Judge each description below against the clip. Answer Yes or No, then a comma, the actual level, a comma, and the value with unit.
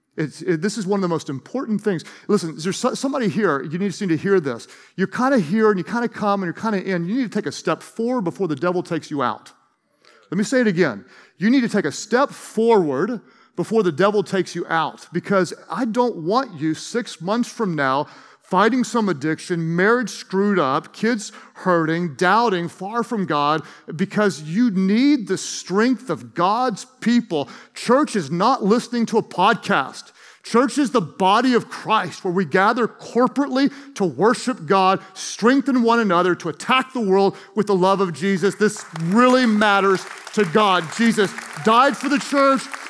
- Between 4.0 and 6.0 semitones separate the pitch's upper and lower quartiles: Yes, average, 4.8 semitones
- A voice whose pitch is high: Yes, high, 200 Hz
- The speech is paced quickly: No, average, 195 wpm